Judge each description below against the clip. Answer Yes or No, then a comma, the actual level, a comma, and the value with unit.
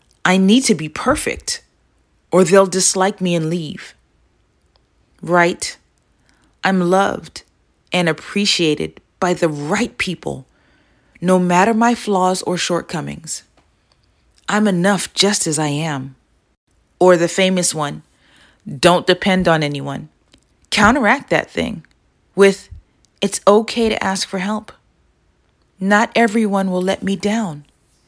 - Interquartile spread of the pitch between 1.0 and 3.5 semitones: No, average, 4.1 semitones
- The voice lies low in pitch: No, medium, 185 Hz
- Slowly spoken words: Yes, slow, 120 wpm